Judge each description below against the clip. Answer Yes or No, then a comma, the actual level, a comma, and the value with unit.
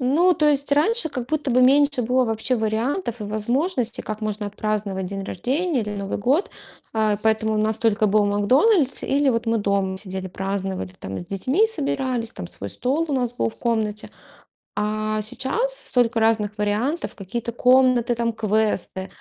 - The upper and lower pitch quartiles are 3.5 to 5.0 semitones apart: Yes, average, 4.1 semitones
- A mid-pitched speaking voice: No, high, 225 Hz